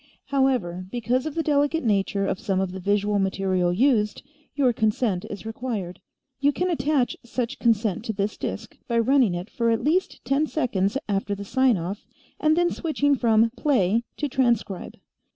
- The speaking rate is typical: Yes, average, 170 wpm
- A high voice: Yes, high, 230 Hz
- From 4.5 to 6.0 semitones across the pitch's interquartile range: Yes, wide, 5.6 semitones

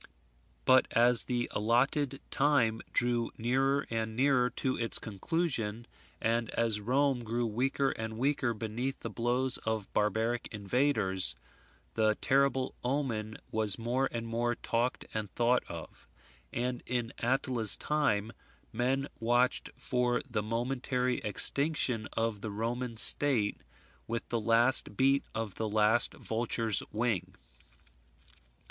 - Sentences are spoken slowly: Yes, slow, 125 wpm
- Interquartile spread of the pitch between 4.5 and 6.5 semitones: No, narrow, 2.6 semitones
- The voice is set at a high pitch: No, low, 120 Hz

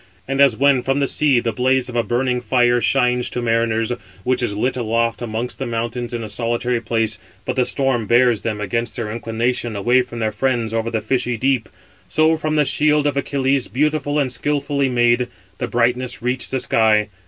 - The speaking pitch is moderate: No, low, 120 Hz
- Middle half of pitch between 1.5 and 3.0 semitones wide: Yes, narrow, 2.4 semitones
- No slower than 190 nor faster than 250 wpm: Yes, average, 200 wpm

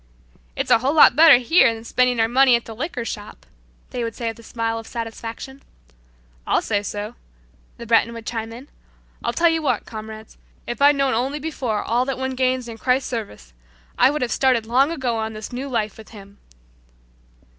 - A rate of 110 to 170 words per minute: No, average, 200 wpm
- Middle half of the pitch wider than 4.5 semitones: No, average, 2.8 semitones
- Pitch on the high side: Yes, high, 235 Hz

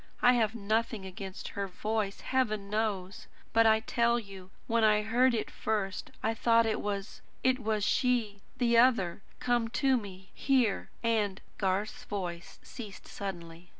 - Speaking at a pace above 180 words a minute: No, average, 155 wpm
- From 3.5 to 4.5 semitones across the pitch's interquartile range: No, average, 2.9 semitones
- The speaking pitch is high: Yes, high, 215 Hz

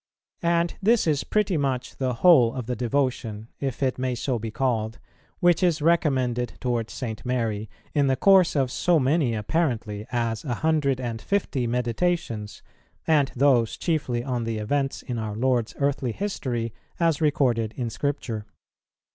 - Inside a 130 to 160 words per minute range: Yes, average, 155 wpm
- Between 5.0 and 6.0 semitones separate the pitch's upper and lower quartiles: No, average, 4.4 semitones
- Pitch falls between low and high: No, low, 130 Hz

